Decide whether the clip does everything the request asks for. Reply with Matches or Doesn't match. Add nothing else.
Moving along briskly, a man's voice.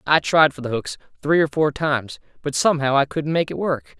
Matches